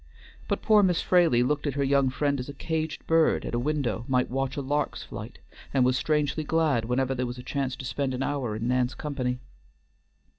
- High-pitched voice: No, low, 135 Hz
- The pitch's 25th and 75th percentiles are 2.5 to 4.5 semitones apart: Yes, average, 3.0 semitones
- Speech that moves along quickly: Yes, fast, 215 wpm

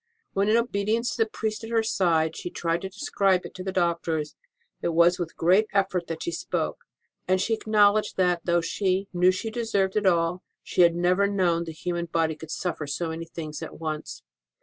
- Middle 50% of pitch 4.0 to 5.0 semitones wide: No, average, 3.2 semitones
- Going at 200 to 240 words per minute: Yes, fast, 205 wpm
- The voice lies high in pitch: No, medium, 180 Hz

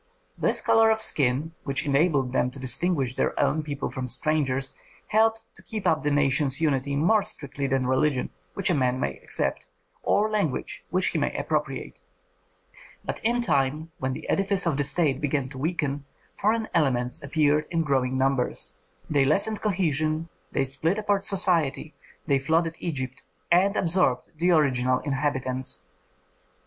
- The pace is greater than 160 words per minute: No, average, 155 wpm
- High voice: No, medium, 150 Hz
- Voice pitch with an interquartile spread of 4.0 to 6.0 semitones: Yes, average, 4.6 semitones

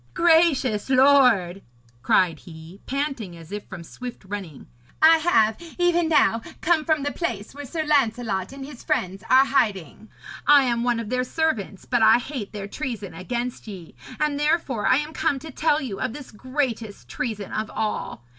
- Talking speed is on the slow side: No, average, 175 wpm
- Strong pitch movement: Yes, wide, 6.1 semitones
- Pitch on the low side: No, high, 245 Hz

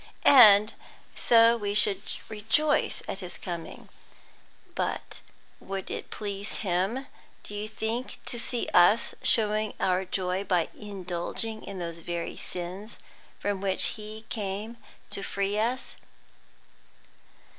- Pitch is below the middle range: No, high, 205 Hz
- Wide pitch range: No, average, 2.9 semitones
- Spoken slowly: Yes, slow, 120 wpm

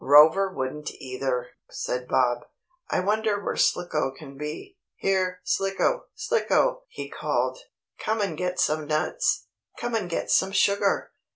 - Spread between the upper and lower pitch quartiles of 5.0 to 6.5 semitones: Yes, wide, 5.4 semitones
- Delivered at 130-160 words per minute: Yes, slow, 135 wpm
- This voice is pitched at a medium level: Yes, medium, 180 Hz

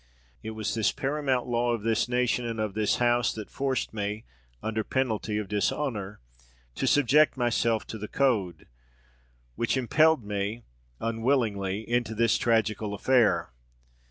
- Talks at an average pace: Yes, average, 145 wpm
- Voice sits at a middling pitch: No, low, 115 Hz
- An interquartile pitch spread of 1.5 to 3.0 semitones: Yes, average, 2.7 semitones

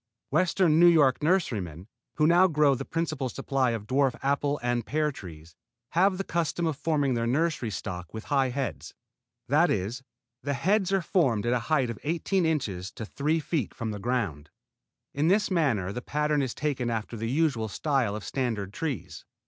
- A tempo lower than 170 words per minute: No, average, 180 wpm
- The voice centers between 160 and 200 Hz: No, low, 135 Hz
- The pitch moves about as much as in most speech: No, wide, 5.8 semitones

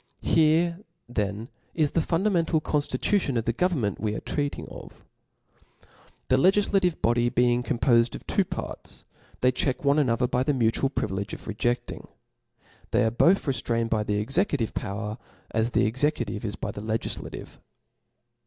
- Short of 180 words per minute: Yes, average, 155 wpm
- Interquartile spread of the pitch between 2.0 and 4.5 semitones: No, average, 5.2 semitones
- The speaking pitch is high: No, low, 125 Hz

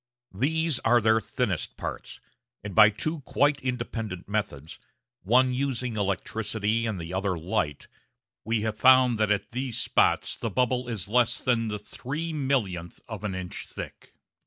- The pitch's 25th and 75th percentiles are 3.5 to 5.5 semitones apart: Yes, average, 3.9 semitones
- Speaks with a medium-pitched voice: No, low, 115 Hz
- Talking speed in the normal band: Yes, average, 155 wpm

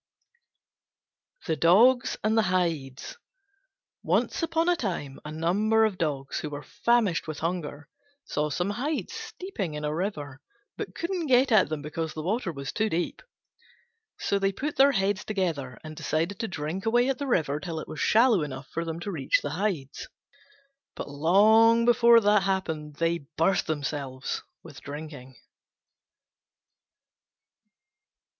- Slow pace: No, average, 150 wpm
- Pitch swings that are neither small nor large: No, wide, 6.5 semitones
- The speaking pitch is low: No, medium, 175 Hz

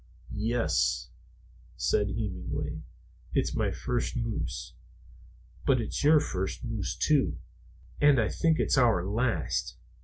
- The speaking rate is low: Yes, slow, 115 wpm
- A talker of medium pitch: No, low, 115 Hz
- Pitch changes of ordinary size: Yes, average, 4.8 semitones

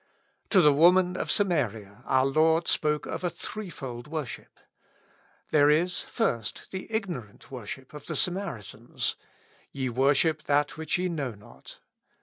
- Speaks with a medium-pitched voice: Yes, medium, 150 Hz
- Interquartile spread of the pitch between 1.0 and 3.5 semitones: No, average, 5.1 semitones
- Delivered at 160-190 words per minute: No, average, 140 wpm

